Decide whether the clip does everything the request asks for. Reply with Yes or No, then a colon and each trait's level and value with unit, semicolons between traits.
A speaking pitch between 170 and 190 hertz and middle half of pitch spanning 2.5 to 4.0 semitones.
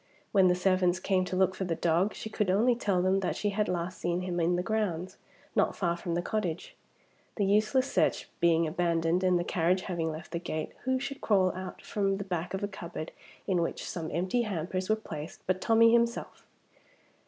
Yes: medium, 185 Hz; average, 2.9 semitones